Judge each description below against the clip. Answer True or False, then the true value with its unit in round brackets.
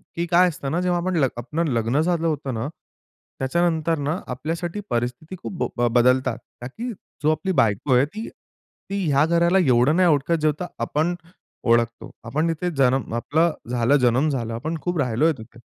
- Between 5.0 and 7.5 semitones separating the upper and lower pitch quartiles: True (5.4 semitones)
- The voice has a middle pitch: True (150 Hz)